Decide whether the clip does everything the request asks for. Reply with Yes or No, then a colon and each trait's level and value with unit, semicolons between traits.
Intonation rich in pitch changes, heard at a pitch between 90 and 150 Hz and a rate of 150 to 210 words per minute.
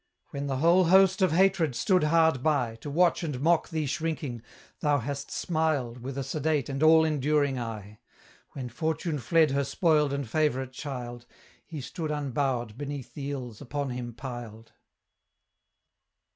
No: average, 3.9 semitones; medium, 140 Hz; average, 155 wpm